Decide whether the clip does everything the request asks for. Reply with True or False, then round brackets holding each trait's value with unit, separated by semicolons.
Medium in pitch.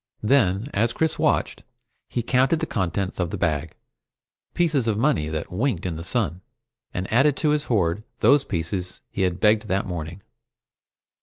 False (100 Hz)